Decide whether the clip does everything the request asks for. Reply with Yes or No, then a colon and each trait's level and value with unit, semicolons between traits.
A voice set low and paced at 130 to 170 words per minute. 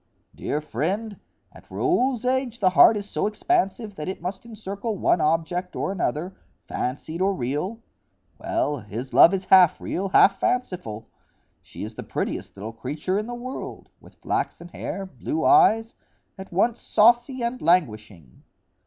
No: high, 190 Hz; average, 150 wpm